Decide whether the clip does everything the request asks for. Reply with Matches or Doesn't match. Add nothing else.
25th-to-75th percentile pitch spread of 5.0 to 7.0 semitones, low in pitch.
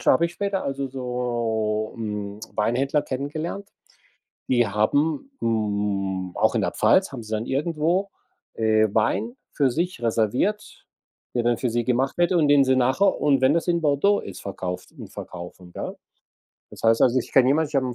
Matches